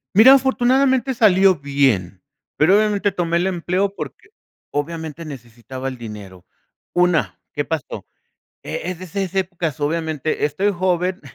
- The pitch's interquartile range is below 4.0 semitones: No, wide, 5.4 semitones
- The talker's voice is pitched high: No, medium, 170 Hz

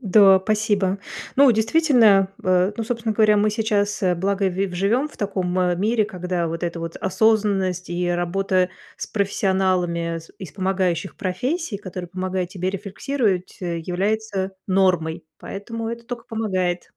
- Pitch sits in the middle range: No, high, 195 Hz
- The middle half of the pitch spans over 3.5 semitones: No, average, 2.9 semitones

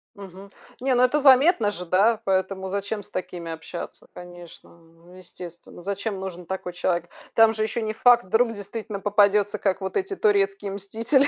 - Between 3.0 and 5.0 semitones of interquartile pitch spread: Yes, average, 3.6 semitones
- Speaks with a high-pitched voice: Yes, high, 200 Hz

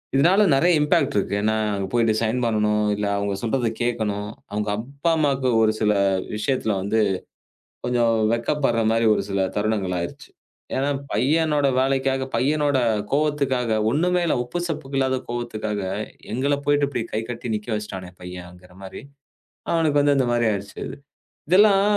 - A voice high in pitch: No, low, 120 Hz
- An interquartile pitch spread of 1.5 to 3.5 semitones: No, average, 5.0 semitones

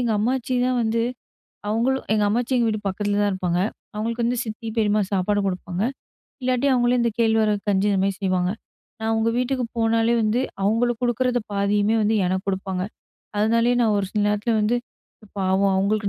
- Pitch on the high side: Yes, high, 215 Hz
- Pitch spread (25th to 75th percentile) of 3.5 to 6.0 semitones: No, average, 2.8 semitones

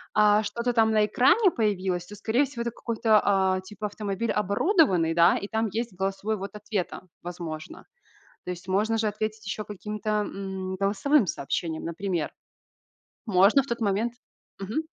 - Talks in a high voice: Yes, high, 210 Hz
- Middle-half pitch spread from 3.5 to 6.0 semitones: No, average, 2.9 semitones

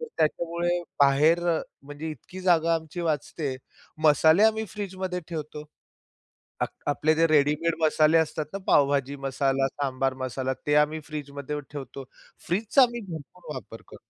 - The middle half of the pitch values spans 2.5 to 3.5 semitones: Yes, average, 3.1 semitones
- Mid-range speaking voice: Yes, medium, 155 Hz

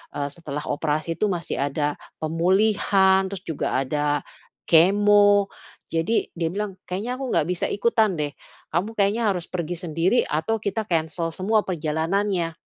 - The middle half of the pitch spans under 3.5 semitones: No, average, 4.3 semitones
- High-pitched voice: No, medium, 180 Hz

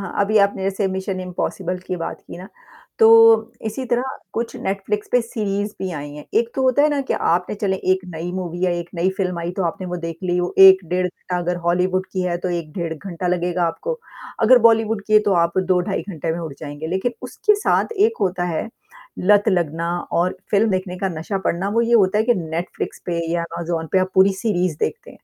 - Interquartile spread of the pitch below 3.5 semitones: Yes, average, 3.0 semitones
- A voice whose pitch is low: No, medium, 185 Hz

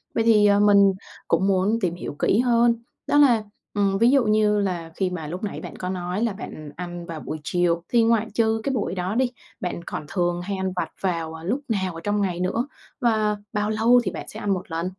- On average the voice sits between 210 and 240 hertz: No, high, 200 Hz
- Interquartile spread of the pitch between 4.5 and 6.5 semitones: No, average, 3.8 semitones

